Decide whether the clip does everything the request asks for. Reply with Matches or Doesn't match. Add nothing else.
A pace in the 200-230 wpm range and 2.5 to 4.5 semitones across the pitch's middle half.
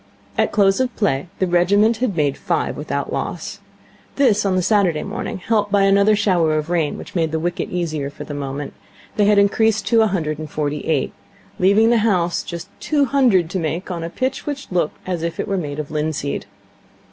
Doesn't match